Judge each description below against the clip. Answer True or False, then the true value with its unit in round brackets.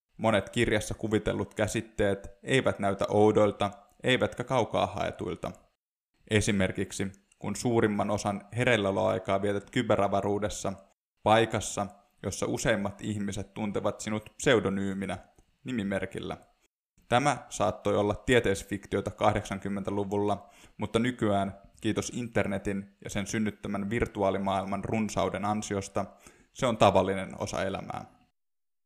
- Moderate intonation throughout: False (1.5 semitones)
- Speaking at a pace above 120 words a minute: False (95 wpm)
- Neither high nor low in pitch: False (100 Hz)